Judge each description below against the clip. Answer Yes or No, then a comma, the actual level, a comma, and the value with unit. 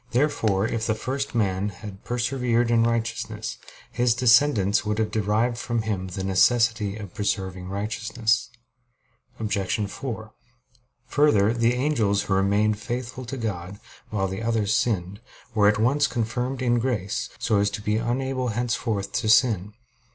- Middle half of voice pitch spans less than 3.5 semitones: Yes, average, 2.9 semitones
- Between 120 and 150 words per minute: Yes, average, 145 wpm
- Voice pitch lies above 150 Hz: No, low, 110 Hz